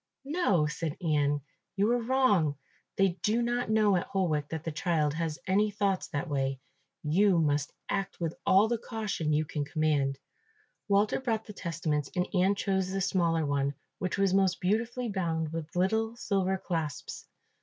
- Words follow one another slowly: No, average, 165 wpm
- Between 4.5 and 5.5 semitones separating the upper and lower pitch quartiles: Yes, average, 4.8 semitones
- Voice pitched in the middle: Yes, medium, 180 Hz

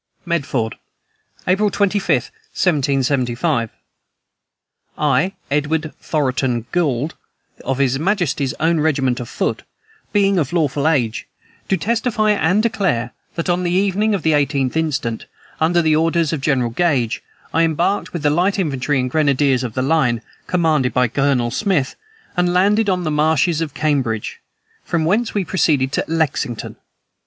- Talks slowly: No, average, 145 wpm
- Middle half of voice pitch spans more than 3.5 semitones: Yes, average, 5.0 semitones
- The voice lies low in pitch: No, medium, 155 Hz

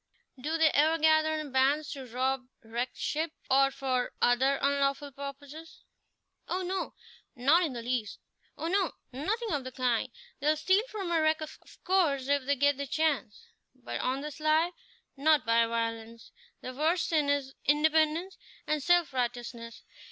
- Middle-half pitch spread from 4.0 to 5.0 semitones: No, average, 3.5 semitones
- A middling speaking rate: Yes, average, 160 wpm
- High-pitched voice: Yes, very high, 285 Hz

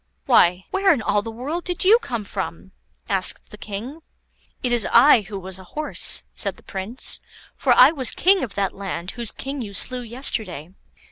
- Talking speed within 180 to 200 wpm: Yes, average, 190 wpm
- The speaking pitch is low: No, high, 230 Hz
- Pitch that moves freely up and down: Yes, wide, 5.8 semitones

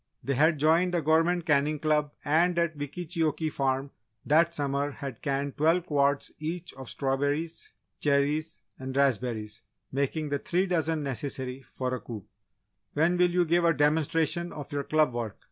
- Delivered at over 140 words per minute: Yes, average, 160 wpm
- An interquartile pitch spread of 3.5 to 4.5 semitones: No, average, 2.8 semitones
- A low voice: No, medium, 150 Hz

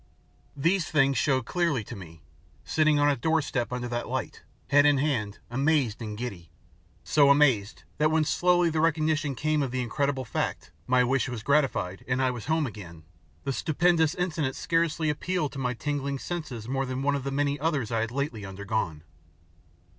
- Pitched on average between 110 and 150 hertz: Yes, medium, 140 Hz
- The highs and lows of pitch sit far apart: No, average, 4.2 semitones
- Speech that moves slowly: No, average, 180 wpm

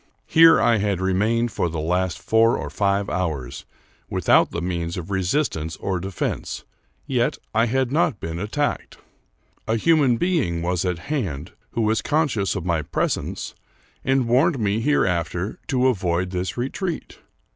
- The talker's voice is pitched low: Yes, low, 100 Hz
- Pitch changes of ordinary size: No, wide, 6.3 semitones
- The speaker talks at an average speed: Yes, average, 155 wpm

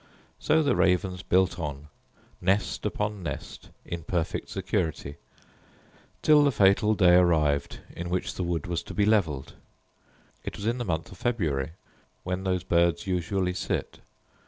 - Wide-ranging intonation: No, average, 3.4 semitones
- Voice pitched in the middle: No, very low, 90 Hz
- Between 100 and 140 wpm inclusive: No, average, 150 wpm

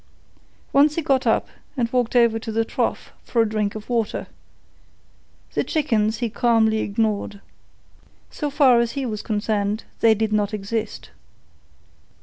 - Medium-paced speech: Yes, average, 145 wpm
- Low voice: No, high, 225 Hz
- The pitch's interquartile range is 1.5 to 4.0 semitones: Yes, narrow, 2.4 semitones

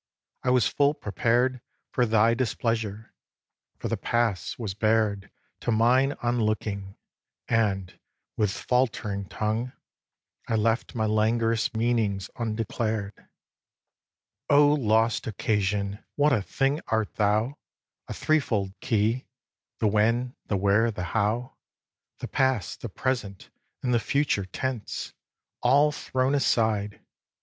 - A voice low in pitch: Yes, low, 115 Hz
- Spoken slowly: Yes, slow, 125 wpm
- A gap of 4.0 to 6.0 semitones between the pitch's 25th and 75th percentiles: No, average, 3.0 semitones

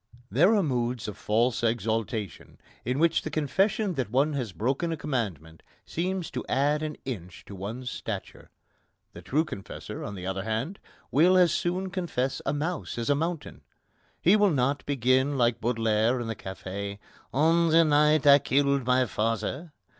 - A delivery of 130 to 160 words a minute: No, average, 170 wpm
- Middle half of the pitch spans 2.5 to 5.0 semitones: No, wide, 5.6 semitones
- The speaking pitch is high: No, low, 135 Hz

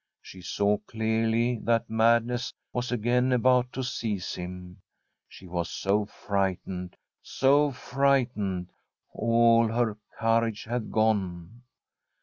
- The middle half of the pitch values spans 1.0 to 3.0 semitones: No, average, 3.7 semitones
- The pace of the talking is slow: Yes, slow, 110 wpm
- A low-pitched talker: Yes, low, 115 Hz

